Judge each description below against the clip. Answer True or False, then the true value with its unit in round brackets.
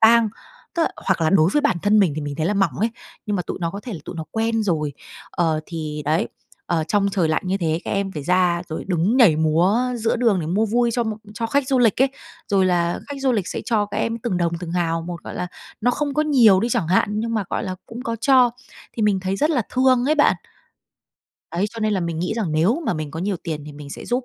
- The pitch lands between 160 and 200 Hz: True (195 Hz)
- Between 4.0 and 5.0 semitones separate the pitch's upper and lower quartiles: False (5.4 semitones)